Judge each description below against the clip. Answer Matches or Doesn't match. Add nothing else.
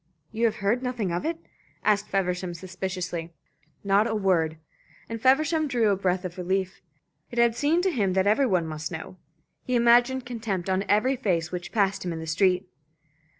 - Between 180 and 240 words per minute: Matches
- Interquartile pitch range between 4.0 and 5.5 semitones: Matches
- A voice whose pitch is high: Matches